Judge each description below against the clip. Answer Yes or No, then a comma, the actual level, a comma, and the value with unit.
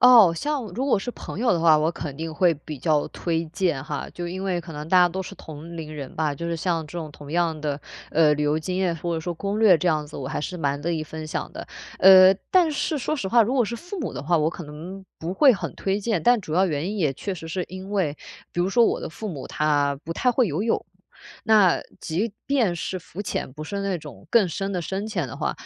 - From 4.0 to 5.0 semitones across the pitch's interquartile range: Yes, average, 4.3 semitones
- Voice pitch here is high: No, medium, 175 Hz